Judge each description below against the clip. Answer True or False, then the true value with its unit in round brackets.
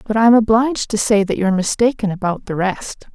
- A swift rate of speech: True (210 wpm)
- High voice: True (210 Hz)